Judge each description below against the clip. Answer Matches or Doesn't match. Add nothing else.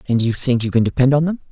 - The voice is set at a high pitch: Doesn't match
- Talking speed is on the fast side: Matches